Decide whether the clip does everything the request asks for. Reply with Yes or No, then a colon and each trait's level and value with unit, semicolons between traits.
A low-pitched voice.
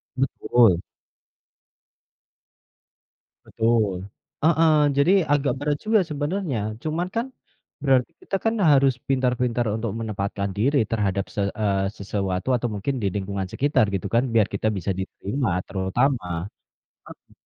Yes: low, 120 Hz